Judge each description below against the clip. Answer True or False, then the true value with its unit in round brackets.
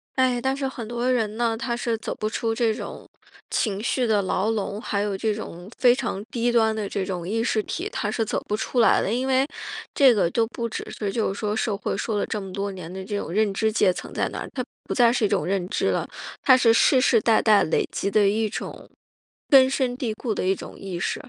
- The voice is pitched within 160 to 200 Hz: False (220 Hz)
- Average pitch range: True (3.1 semitones)